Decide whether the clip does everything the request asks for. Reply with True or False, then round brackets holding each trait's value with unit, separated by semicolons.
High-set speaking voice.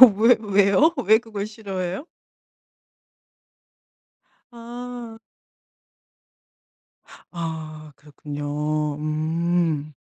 False (175 Hz)